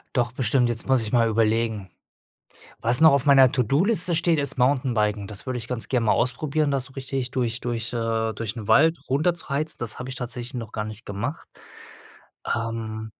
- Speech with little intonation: No, average, 3.3 semitones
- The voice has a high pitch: No, low, 120 Hz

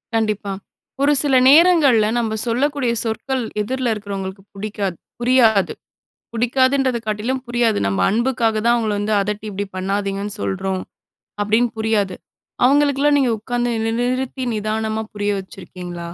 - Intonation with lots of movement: No, average, 3.9 semitones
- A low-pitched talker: No, high, 220 Hz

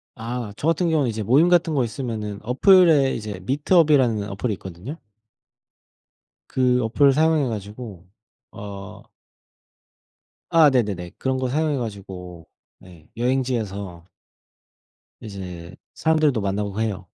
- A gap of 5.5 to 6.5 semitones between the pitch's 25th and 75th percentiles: Yes, wide, 5.9 semitones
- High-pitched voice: No, low, 115 Hz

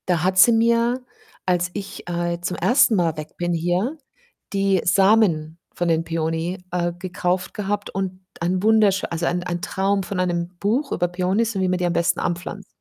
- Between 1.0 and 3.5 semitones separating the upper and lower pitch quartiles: Yes, narrow, 2.4 semitones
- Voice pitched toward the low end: No, medium, 180 Hz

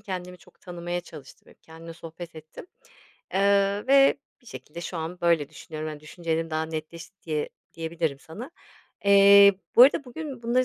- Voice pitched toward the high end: No, medium, 170 Hz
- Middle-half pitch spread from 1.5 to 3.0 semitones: No, average, 3.9 semitones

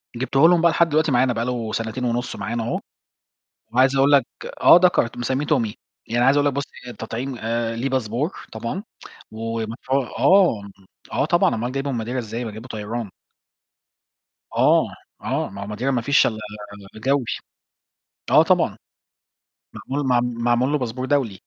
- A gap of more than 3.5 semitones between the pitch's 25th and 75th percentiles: No, average, 3.2 semitones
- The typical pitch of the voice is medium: No, low, 125 Hz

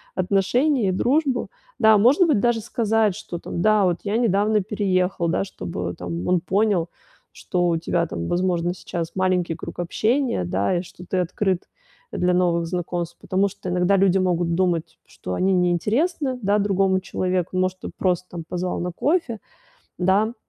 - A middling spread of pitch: Yes, average, 3.2 semitones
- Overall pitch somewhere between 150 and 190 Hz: Yes, medium, 185 Hz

